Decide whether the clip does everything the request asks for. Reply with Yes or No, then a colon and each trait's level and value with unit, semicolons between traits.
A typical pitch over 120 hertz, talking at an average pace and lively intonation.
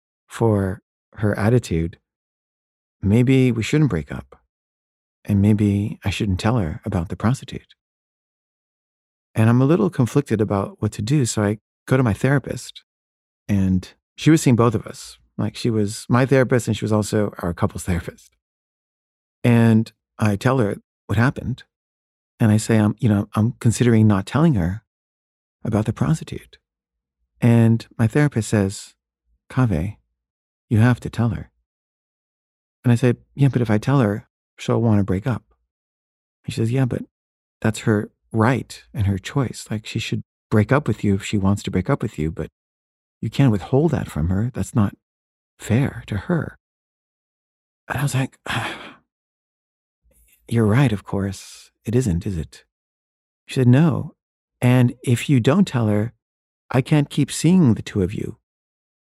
No: low, 105 Hz; average, 165 wpm; wide, 6.4 semitones